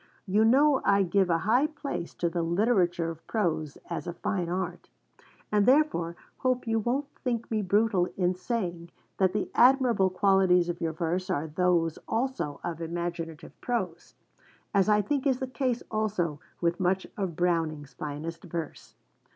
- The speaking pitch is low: No, medium, 185 Hz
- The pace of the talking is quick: No, average, 160 wpm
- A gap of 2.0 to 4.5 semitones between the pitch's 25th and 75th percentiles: No, average, 4.9 semitones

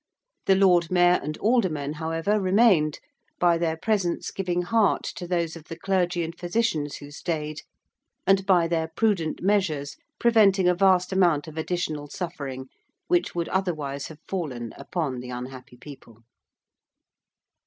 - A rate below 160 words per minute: Yes, average, 145 wpm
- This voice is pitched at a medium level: Yes, medium, 170 Hz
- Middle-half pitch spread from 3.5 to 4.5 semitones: Yes, average, 3.8 semitones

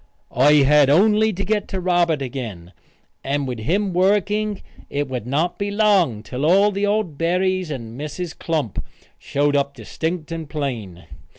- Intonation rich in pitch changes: Yes, wide, 5.8 semitones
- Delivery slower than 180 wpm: Yes, average, 155 wpm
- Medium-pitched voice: Yes, medium, 160 Hz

